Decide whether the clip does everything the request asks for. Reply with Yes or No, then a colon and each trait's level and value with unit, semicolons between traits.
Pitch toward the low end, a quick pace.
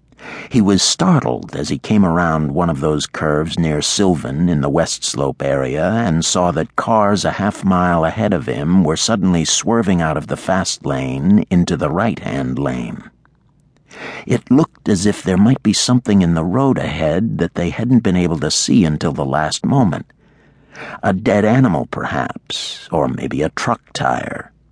No: very low, 85 Hz; average, 175 wpm